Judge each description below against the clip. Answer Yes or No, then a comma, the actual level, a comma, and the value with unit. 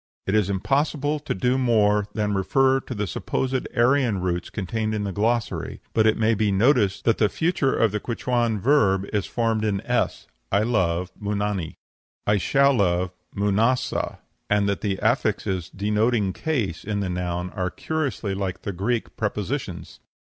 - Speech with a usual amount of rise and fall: Yes, average, 3.8 semitones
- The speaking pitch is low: Yes, low, 105 Hz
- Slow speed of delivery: No, average, 165 wpm